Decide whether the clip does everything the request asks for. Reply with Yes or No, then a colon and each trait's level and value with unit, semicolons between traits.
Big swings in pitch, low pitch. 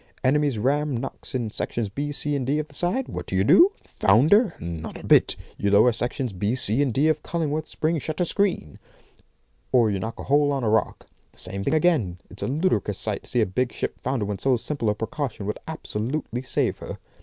Yes: wide, 5.9 semitones; low, 130 Hz